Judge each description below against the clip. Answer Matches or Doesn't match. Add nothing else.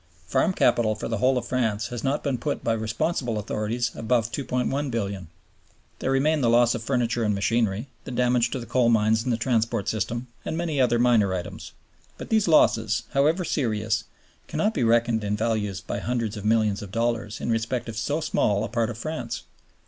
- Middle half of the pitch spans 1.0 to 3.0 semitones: Matches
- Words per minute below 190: Doesn't match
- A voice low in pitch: Matches